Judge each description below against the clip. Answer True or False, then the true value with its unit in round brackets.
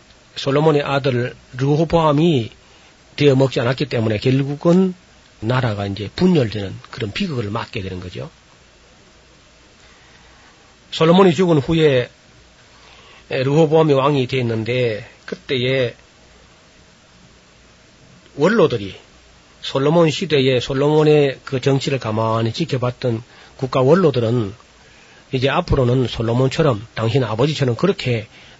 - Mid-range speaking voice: False (130 Hz)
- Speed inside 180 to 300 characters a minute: True (250 characters per minute)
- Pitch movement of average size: True (4.5 semitones)